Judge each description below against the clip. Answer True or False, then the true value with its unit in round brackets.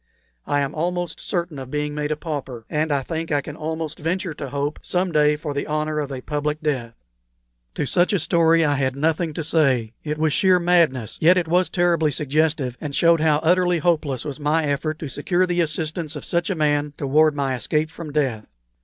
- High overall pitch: False (155 Hz)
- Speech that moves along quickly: True (210 wpm)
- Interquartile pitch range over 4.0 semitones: False (2.4 semitones)